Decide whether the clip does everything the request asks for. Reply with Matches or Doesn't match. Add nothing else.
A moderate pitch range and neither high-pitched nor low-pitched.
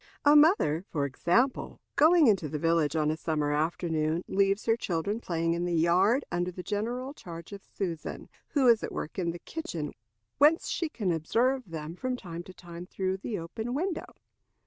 Doesn't match